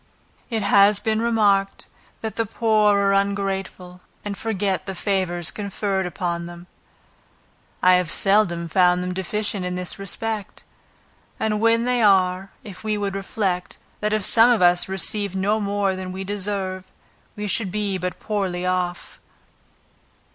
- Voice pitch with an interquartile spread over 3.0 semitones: No, narrow, 2.4 semitones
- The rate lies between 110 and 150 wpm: Yes, average, 145 wpm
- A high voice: Yes, high, 195 Hz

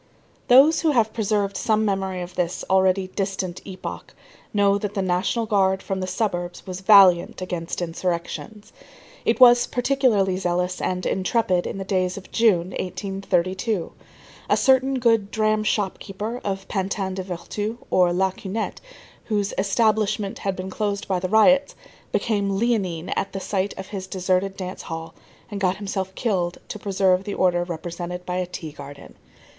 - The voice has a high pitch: Yes, high, 195 Hz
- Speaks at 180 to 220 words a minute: No, average, 160 wpm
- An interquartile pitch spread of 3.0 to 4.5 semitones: No, narrow, 2.5 semitones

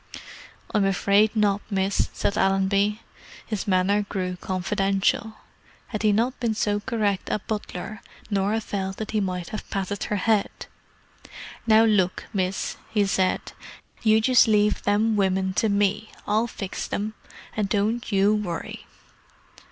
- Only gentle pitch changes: Yes, narrow, 1.9 semitones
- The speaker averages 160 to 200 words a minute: No, average, 140 wpm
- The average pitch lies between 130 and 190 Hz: No, high, 205 Hz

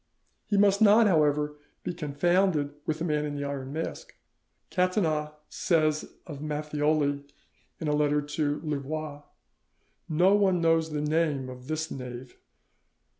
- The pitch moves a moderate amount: No, narrow, 2.3 semitones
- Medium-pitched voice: Yes, medium, 150 Hz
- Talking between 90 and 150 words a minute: Yes, slow, 135 wpm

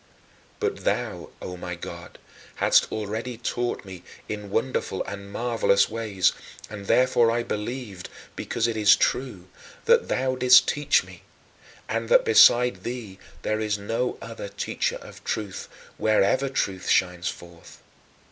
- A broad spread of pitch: No, average, 3.8 semitones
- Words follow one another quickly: No, average, 140 wpm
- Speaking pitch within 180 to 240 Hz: No, low, 110 Hz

